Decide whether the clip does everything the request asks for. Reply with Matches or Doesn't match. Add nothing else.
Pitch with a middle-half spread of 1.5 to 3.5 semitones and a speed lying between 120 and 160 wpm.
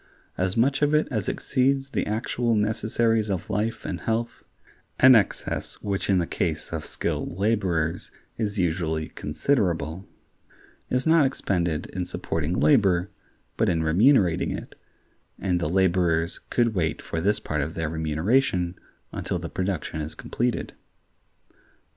Doesn't match